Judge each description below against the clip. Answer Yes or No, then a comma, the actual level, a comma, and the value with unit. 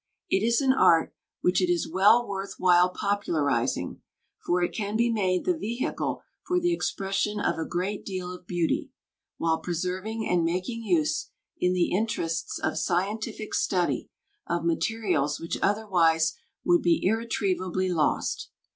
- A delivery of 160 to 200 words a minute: No, average, 145 wpm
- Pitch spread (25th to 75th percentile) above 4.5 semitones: No, average, 3.6 semitones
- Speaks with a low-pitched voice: No, medium, 185 Hz